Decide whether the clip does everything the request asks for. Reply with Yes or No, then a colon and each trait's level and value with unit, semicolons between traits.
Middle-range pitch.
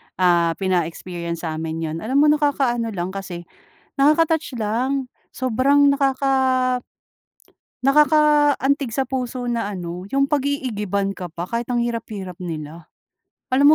No: high, 235 Hz